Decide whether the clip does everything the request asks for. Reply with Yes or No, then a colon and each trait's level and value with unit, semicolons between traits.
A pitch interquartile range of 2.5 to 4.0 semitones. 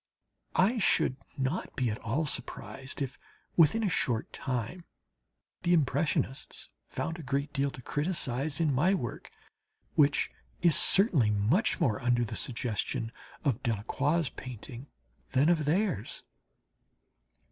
No: average, 5.1 semitones